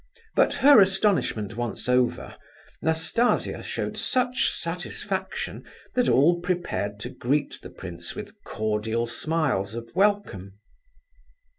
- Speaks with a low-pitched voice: No, medium, 150 Hz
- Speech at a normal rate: No, slow, 110 wpm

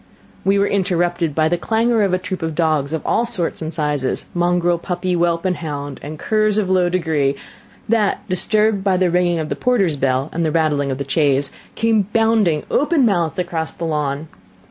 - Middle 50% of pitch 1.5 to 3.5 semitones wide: No, average, 4.0 semitones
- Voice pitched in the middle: Yes, medium, 175 Hz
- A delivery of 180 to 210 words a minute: Yes, average, 195 wpm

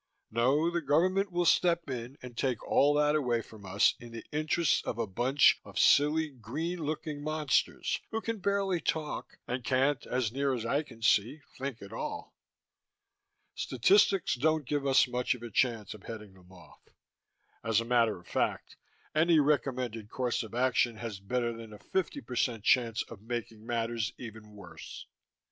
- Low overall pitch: Yes, low, 125 Hz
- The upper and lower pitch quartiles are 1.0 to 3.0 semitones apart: No, average, 4.6 semitones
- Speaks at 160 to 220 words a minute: Yes, average, 170 wpm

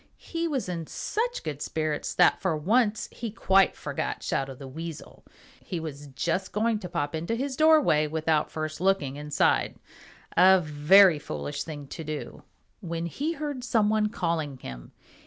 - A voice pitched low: No, medium, 170 Hz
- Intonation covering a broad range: Yes, wide, 6.3 semitones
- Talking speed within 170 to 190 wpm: No, average, 160 wpm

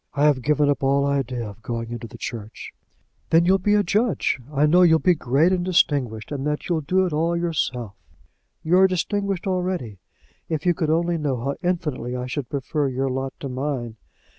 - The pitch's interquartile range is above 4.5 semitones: Yes, wide, 5.4 semitones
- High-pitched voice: No, medium, 150 Hz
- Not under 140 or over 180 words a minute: No, average, 200 wpm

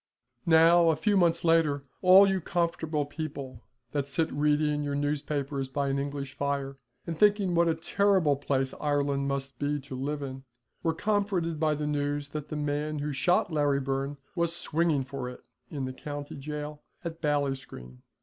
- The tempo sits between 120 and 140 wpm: No, average, 170 wpm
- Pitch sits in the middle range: Yes, medium, 145 Hz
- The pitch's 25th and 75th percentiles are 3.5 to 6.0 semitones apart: No, average, 2.7 semitones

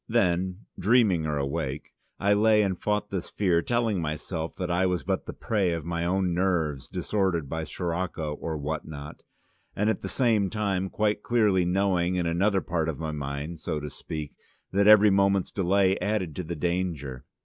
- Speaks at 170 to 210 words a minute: Yes, average, 180 wpm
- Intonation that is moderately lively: Yes, average, 3.9 semitones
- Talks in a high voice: No, very low, 90 Hz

